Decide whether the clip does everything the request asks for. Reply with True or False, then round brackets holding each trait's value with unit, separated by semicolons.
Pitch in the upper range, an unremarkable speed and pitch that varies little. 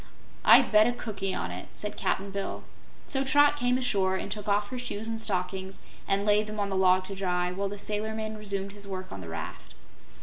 False (200 Hz; 225 wpm; 2.3 semitones)